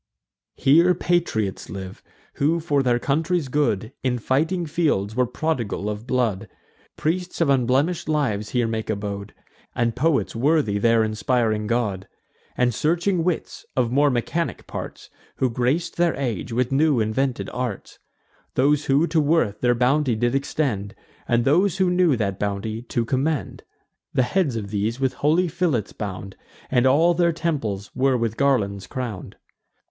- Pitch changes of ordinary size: No, wide, 5.9 semitones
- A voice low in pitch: Yes, low, 130 Hz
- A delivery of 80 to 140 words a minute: No, average, 150 wpm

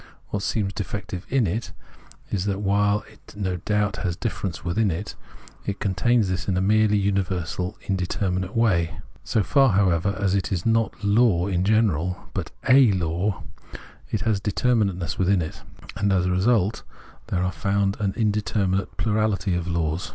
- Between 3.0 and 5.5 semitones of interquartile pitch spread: No, narrow, 2.6 semitones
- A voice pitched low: Yes, low, 100 Hz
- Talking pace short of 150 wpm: No, average, 165 wpm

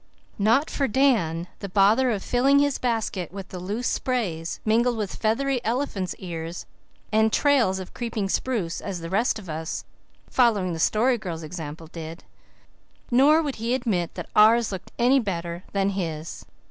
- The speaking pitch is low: No, high, 210 Hz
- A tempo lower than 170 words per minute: Yes, average, 160 wpm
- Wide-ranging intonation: Yes, wide, 5.7 semitones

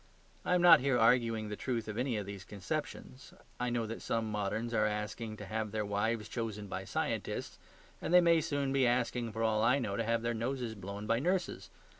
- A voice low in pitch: Yes, low, 115 Hz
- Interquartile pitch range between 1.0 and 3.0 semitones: Yes, average, 2.7 semitones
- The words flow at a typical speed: No, fast, 215 wpm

